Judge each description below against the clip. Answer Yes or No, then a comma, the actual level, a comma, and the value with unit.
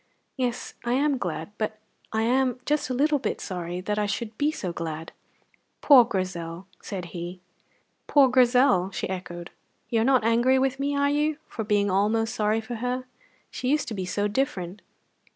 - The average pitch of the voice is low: No, high, 225 Hz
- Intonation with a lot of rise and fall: Yes, wide, 5.7 semitones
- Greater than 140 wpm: Yes, average, 180 wpm